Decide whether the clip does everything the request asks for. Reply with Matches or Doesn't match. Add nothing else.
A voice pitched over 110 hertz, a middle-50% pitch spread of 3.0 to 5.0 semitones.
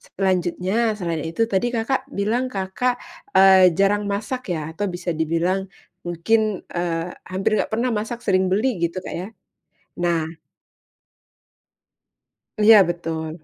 Matches